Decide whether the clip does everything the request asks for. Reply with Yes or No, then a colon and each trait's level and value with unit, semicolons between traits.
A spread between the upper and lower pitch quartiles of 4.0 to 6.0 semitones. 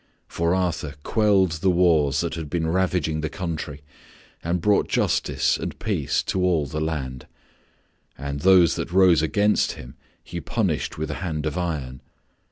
No: average, 3.3 semitones